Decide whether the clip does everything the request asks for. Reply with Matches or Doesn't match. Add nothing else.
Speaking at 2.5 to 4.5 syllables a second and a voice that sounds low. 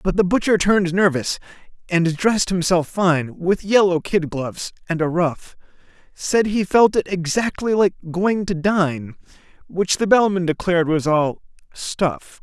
Doesn't match